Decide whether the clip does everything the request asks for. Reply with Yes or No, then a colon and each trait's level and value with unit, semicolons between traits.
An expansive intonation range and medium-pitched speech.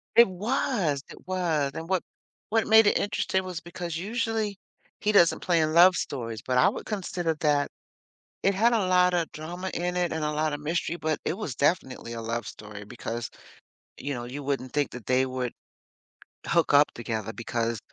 Yes: wide, 6.1 semitones; medium, 160 Hz